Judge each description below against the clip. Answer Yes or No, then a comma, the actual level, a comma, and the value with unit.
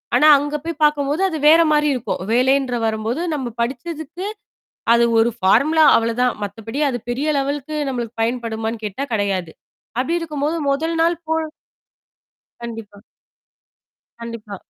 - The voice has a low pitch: No, very high, 255 Hz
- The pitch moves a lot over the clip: No, average, 4.9 semitones